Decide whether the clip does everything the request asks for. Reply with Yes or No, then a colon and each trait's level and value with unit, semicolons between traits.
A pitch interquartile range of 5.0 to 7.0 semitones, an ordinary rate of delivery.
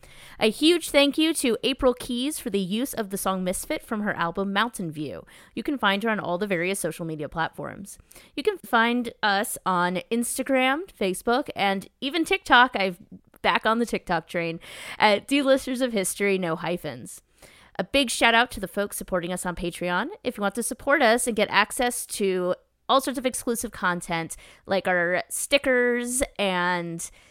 Yes: wide, 5.6 semitones; average, 180 wpm